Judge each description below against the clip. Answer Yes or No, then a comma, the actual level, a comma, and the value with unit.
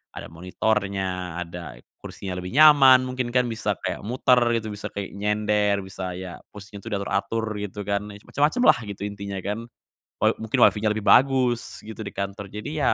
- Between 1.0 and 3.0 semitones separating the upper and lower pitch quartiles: Yes, average, 2.7 semitones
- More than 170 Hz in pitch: No, low, 105 Hz